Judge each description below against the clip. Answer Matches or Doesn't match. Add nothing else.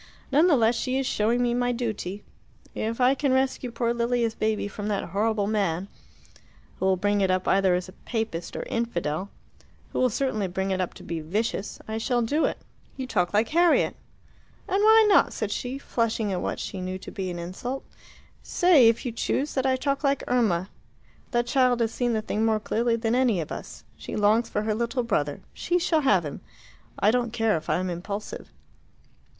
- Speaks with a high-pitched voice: Matches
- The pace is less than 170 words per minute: Doesn't match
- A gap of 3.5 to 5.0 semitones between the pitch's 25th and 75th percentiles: Matches